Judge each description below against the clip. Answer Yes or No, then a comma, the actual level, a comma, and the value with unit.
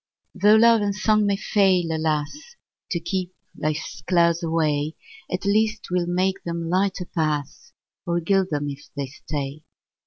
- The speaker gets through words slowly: No, average, 150 wpm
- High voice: No, medium, 175 Hz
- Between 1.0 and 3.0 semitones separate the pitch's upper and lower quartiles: No, average, 4.2 semitones